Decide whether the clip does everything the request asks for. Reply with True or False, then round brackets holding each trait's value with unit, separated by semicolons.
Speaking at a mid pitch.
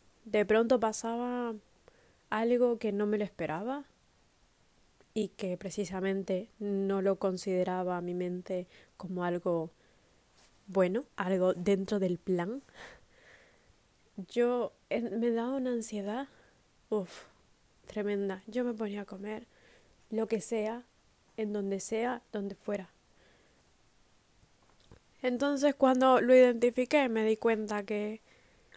False (210 Hz)